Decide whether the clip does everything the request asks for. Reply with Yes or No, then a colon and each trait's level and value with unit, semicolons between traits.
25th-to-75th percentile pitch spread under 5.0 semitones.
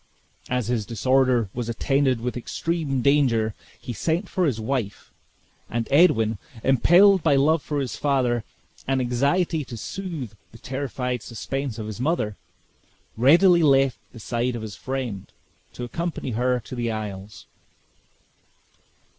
Yes: average, 3.7 semitones